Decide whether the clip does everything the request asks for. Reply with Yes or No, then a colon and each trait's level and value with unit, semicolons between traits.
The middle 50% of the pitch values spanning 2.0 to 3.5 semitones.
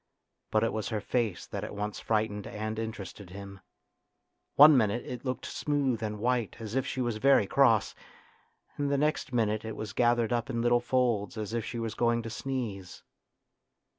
Yes: average, 2.7 semitones